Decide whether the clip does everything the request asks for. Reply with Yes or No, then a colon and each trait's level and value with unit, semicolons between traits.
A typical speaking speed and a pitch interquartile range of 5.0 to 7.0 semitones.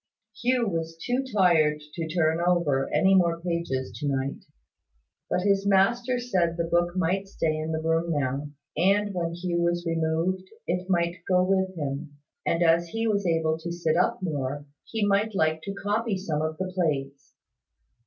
No: average, 175 wpm; average, 3.2 semitones